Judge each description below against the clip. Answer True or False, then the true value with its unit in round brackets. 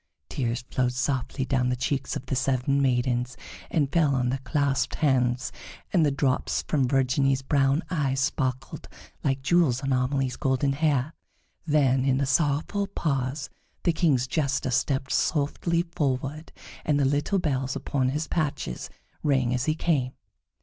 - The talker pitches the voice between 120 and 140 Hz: True (135 Hz)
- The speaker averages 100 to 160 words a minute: True (150 wpm)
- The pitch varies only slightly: True (2.3 semitones)